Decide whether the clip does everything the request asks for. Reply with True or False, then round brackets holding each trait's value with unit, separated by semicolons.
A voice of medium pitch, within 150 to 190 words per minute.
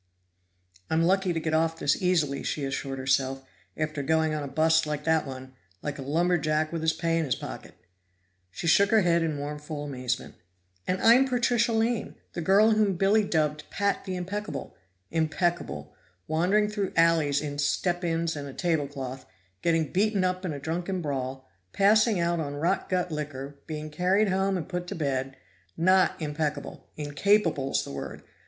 True (160 Hz; 175 wpm)